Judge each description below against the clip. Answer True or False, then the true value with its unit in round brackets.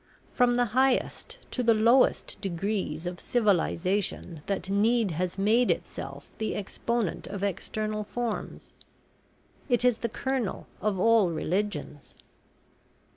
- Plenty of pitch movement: False (3.9 semitones)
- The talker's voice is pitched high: True (210 Hz)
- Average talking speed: False (120 wpm)